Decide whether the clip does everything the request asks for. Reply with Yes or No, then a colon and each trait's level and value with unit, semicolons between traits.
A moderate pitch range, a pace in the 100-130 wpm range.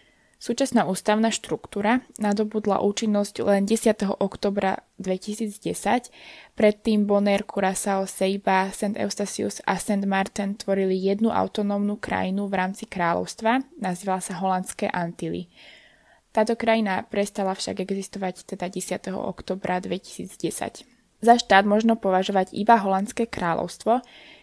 No: narrow, 2.3 semitones; slow, 110 wpm